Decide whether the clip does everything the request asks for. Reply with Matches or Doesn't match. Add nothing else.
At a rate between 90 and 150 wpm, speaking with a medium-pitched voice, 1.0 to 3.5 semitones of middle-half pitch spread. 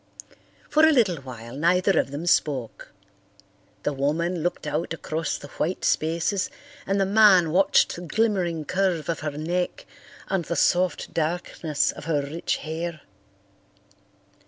Matches